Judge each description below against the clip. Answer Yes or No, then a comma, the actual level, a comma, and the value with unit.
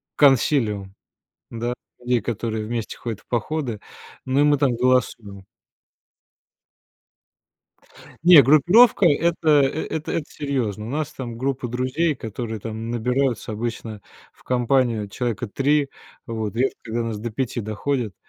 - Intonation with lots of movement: No, average, 3.8 semitones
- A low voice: Yes, low, 120 Hz